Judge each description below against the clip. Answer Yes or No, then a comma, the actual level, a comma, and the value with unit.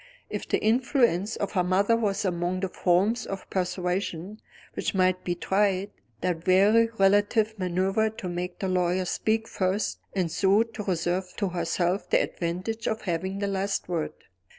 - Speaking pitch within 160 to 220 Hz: Yes, high, 190 Hz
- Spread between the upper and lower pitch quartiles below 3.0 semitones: Yes, narrow, 2.5 semitones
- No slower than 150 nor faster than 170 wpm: Yes, average, 160 wpm